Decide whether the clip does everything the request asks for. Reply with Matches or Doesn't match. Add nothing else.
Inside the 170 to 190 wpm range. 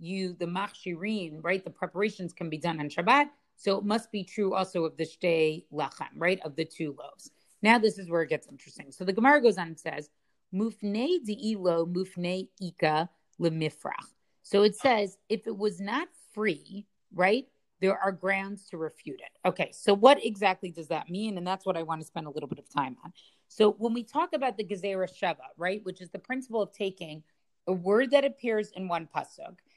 Doesn't match